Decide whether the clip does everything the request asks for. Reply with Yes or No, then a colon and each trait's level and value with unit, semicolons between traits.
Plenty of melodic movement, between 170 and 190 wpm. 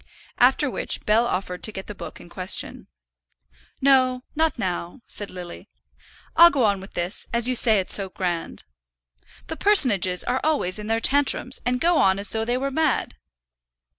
Yes: wide, 5.8 semitones; average, 175 wpm